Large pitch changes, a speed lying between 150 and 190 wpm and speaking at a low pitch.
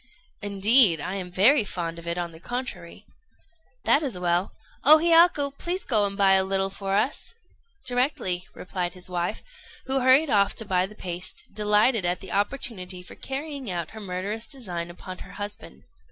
No: wide, 5.8 semitones; average, 175 wpm; high, 200 Hz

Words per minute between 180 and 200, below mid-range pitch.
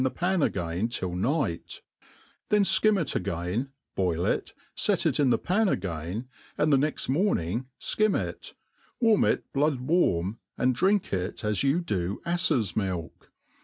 No: average, 155 wpm; low, 125 Hz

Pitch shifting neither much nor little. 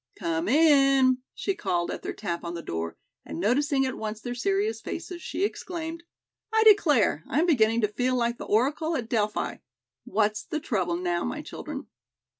No: wide, 7.2 semitones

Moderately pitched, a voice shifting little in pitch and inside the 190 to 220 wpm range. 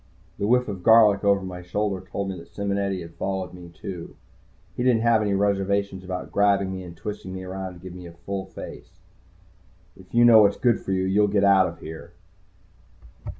No: very low, 95 Hz; narrow, 1.7 semitones; fast, 205 wpm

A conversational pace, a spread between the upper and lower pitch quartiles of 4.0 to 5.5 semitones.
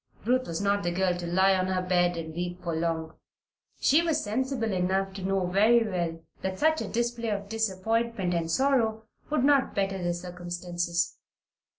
Yes: average, 180 wpm; average, 4.3 semitones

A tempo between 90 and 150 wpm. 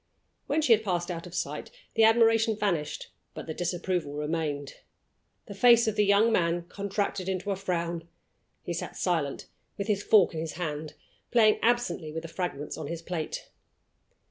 No: average, 170 wpm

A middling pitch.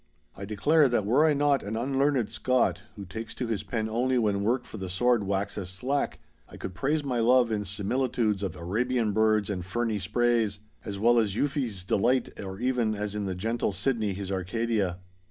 No: low, 110 Hz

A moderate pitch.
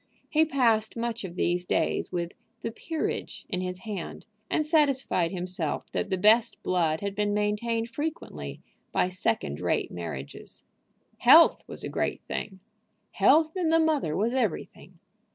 No: high, 210 Hz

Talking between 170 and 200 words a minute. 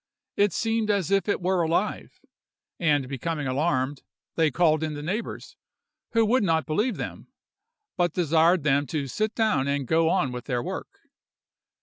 No: average, 160 wpm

